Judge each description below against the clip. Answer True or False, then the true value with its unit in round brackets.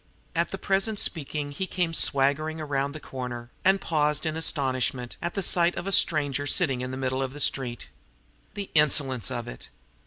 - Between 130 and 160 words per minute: False (185 wpm)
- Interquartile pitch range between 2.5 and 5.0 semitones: True (3.9 semitones)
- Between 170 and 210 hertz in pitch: False (145 Hz)